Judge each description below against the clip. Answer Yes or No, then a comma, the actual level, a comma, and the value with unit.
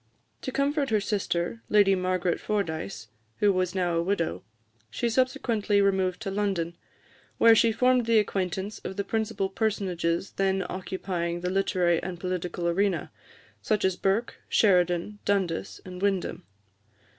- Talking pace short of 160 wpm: Yes, average, 140 wpm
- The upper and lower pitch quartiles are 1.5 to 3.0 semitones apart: Yes, average, 2.7 semitones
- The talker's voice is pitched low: No, high, 190 Hz